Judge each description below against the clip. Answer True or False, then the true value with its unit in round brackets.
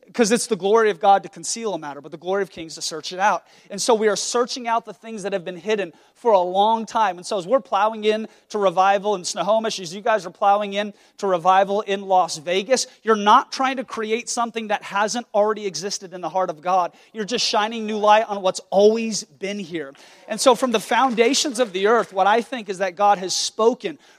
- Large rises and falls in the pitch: False (3.0 semitones)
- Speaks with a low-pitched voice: False (210 Hz)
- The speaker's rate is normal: False (240 wpm)